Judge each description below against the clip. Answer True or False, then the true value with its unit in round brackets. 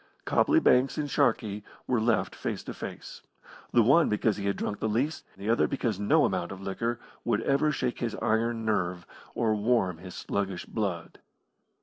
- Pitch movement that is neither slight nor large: True (3.6 semitones)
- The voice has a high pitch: False (110 Hz)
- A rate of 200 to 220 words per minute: False (180 wpm)